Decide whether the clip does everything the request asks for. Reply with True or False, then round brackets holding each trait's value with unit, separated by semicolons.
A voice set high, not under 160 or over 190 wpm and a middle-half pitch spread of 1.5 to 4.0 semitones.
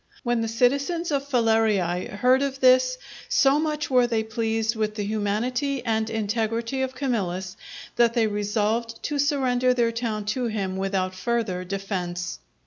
False (230 Hz; 150 wpm; 3.5 semitones)